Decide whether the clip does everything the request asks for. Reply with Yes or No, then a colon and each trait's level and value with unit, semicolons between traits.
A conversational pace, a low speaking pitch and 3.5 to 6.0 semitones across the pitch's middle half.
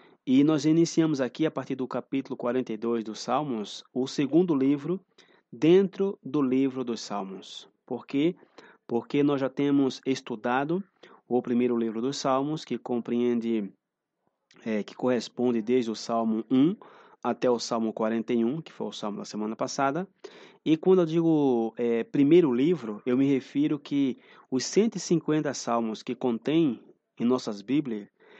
Yes: average, 150 wpm; low, 130 Hz; average, 4.6 semitones